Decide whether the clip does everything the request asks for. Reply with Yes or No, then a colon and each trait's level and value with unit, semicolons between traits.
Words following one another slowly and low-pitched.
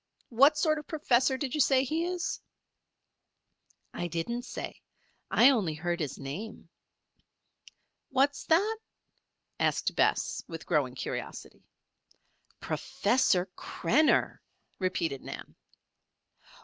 No: slow, 100 wpm; very high, 255 Hz